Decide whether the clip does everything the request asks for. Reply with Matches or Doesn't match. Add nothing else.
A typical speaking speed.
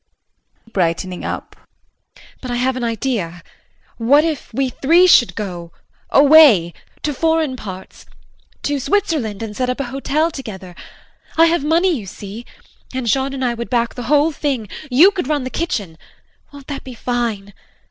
Matches